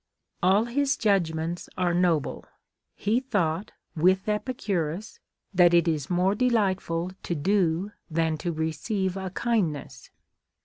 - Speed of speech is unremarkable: No, slow, 125 wpm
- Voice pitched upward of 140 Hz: Yes, medium, 185 Hz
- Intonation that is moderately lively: Yes, average, 3.9 semitones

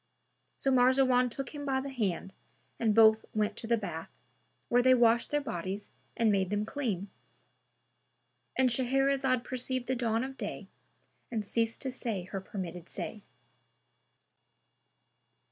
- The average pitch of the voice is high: Yes, high, 235 Hz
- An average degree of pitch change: Yes, average, 3.8 semitones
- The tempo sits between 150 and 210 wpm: No, average, 140 wpm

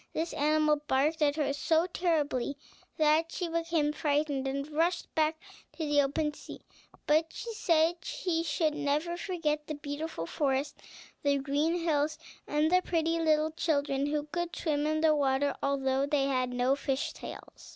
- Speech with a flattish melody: Yes, narrow, 2.3 semitones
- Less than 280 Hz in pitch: No, very high, 300 Hz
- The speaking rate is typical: Yes, average, 160 wpm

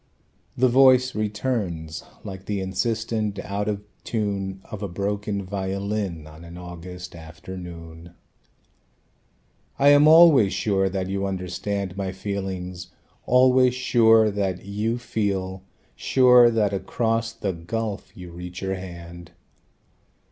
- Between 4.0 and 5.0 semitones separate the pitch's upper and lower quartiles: No, average, 3.6 semitones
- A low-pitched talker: Yes, low, 100 Hz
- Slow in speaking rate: Yes, slow, 120 wpm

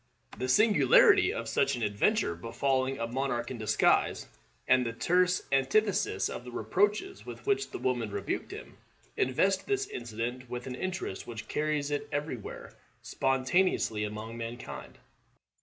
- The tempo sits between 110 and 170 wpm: Yes, average, 145 wpm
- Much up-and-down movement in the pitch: Yes, wide, 7.8 semitones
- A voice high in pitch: No, low, 130 Hz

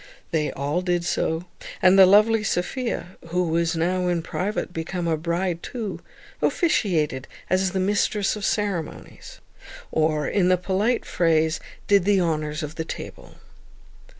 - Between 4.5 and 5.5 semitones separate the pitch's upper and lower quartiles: No, average, 3.2 semitones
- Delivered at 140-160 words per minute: Yes, average, 150 wpm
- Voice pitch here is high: No, medium, 180 Hz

